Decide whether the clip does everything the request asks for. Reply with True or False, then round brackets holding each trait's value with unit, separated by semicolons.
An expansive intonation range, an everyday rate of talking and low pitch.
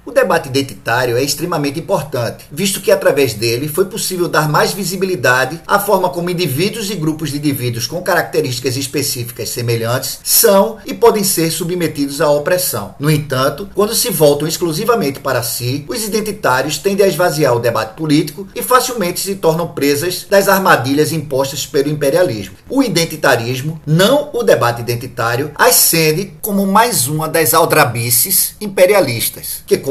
False (5.8 semitones; 150 wpm; 160 Hz)